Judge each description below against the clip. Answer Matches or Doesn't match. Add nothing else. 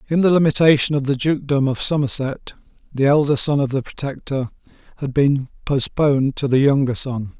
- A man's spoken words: Matches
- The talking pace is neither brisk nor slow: Matches